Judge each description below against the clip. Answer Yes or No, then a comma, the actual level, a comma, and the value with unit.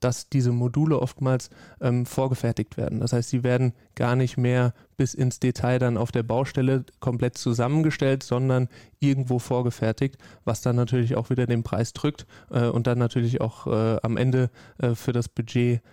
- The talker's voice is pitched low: Yes, low, 125 Hz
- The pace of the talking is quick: No, average, 175 wpm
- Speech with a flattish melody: Yes, narrow, 1.4 semitones